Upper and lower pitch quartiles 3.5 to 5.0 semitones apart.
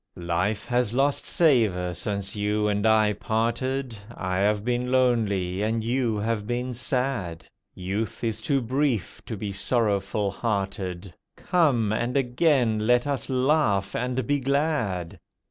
Yes: average, 4.1 semitones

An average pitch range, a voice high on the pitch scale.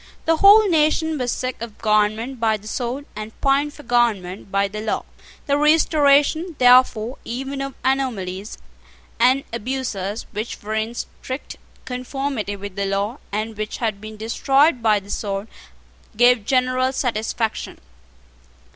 Yes: average, 4.2 semitones; high, 240 Hz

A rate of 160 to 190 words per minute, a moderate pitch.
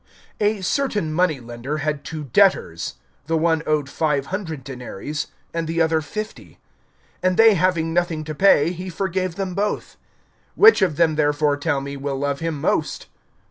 Yes: average, 165 wpm; medium, 160 Hz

